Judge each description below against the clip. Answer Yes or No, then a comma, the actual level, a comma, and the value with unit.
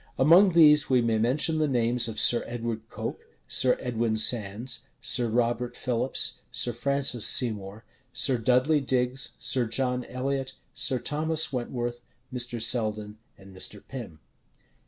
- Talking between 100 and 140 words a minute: Yes, slow, 135 wpm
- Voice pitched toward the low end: Yes, low, 125 Hz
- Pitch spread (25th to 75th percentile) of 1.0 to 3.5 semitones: Yes, narrow, 2.5 semitones